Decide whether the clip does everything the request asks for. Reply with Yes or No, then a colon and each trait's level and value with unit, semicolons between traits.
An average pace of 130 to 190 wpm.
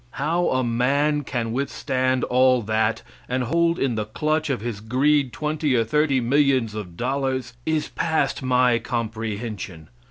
Yes: average, 150 wpm